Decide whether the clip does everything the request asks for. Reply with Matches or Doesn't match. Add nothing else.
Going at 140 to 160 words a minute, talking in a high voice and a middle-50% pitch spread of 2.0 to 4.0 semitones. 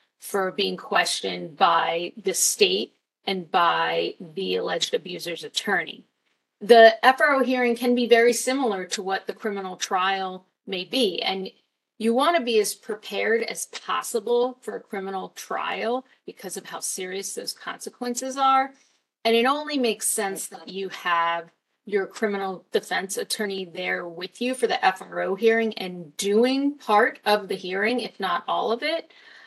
Doesn't match